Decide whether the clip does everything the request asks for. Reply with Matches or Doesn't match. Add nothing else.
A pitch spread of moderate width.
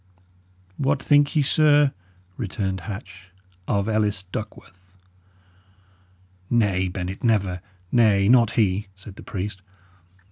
Matches